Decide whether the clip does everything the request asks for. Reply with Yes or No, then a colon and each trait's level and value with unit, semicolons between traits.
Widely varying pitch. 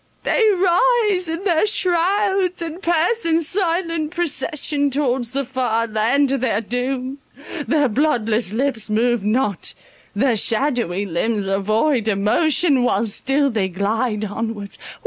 Yes: wide, 6.8 semitones